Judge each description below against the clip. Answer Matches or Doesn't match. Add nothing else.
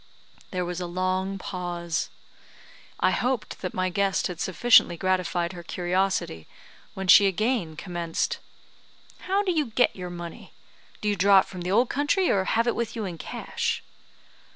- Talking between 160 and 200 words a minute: Matches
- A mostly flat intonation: Doesn't match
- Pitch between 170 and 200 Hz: Matches